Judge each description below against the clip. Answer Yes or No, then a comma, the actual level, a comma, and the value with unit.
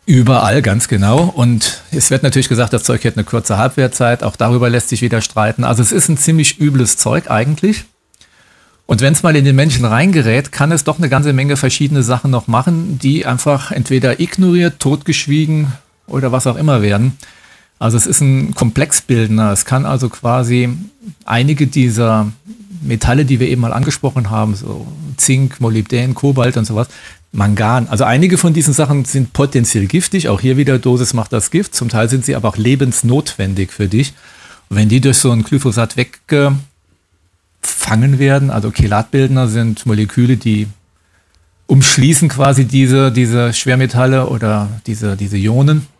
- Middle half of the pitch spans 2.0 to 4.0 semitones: Yes, average, 3.7 semitones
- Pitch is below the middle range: Yes, low, 130 Hz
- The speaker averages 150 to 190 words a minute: Yes, average, 170 wpm